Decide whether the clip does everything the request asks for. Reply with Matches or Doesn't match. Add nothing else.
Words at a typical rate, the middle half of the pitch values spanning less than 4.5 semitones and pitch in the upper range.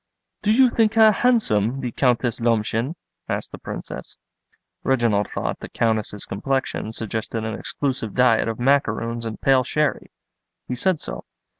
Doesn't match